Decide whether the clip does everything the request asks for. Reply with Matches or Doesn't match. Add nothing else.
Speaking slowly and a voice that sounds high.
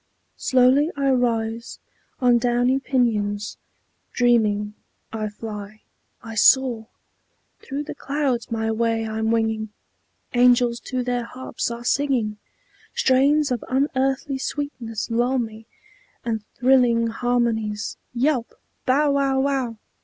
Matches